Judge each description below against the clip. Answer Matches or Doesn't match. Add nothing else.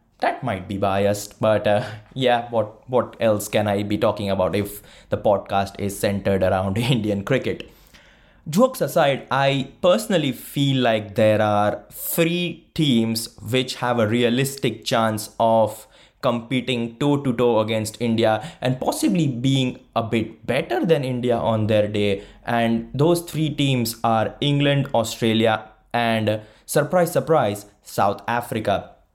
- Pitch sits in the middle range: Doesn't match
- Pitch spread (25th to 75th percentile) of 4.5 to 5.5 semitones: Doesn't match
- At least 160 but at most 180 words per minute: Doesn't match